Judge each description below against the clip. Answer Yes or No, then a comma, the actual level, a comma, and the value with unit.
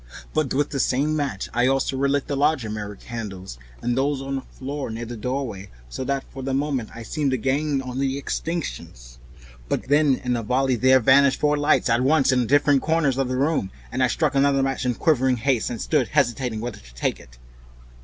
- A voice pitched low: Yes, low, 130 Hz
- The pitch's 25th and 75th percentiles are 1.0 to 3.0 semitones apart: Yes, average, 2.7 semitones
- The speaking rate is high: Yes, fast, 215 wpm